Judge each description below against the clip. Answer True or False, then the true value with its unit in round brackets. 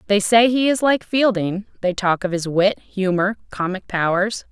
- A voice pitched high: True (200 Hz)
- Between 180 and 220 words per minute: True (185 wpm)